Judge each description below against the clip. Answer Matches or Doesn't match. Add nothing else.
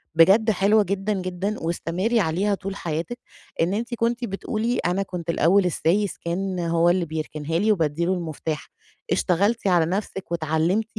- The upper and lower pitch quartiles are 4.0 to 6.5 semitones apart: Doesn't match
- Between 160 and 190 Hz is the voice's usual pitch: Matches